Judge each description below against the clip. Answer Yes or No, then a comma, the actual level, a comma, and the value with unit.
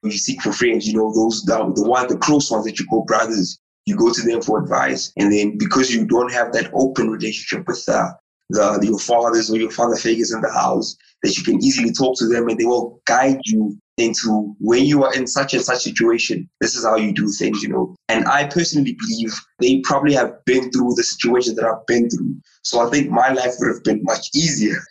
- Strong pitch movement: No, average, 2.9 semitones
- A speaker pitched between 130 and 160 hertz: No, low, 120 Hz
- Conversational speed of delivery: No, fast, 240 wpm